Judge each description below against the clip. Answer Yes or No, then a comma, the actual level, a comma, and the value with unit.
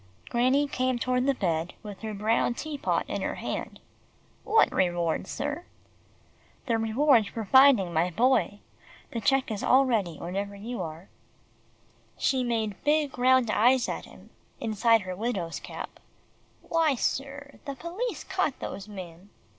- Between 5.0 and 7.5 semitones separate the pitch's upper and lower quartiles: Yes, wide, 5.4 semitones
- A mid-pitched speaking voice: No, high, 235 Hz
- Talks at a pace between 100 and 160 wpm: Yes, average, 145 wpm